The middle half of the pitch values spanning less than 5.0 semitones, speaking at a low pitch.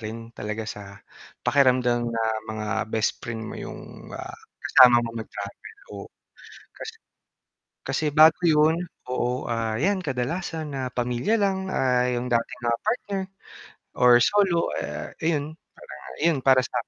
No: wide, 5.4 semitones; low, 125 Hz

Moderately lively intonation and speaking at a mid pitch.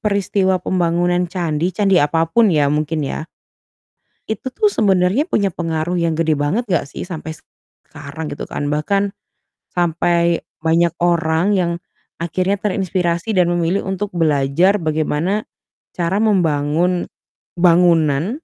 Yes: average, 3.1 semitones; medium, 175 Hz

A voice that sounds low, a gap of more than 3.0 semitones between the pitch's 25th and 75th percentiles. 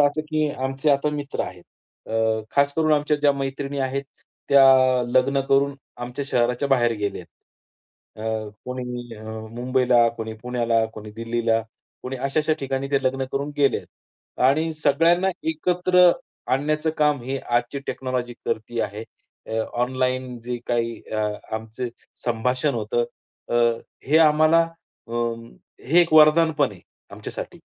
Yes: low, 130 Hz; average, 3.5 semitones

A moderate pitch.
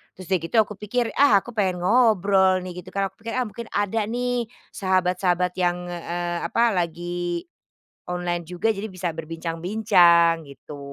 Yes: medium, 180 Hz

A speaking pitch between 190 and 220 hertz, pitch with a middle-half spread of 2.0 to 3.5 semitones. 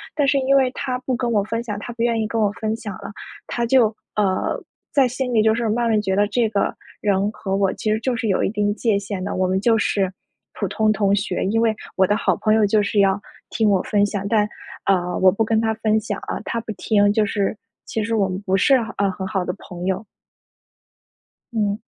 Yes: high, 210 Hz; narrow, 2.4 semitones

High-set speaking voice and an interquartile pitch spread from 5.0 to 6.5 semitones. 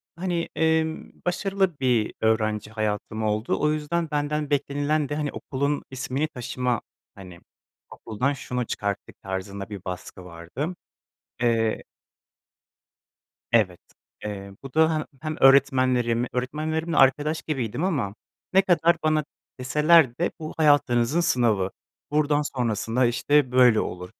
No: low, 130 Hz; wide, 5.6 semitones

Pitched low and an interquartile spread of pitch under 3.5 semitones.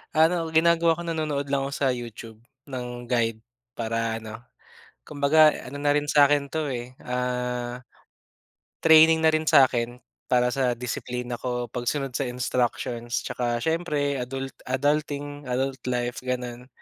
Yes: low, 130 Hz; average, 3.1 semitones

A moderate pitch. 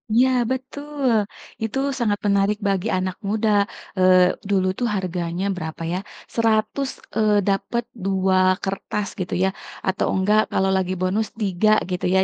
No: high, 195 Hz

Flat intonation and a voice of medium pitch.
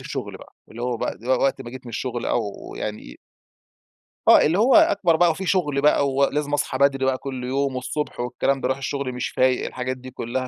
No: narrow, 2.3 semitones; low, 130 Hz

